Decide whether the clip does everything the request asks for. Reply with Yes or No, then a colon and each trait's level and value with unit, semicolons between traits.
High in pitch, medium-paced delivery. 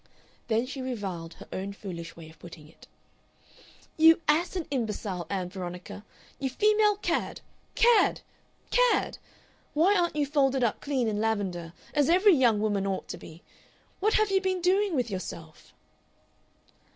Yes: high, 240 Hz; average, 150 wpm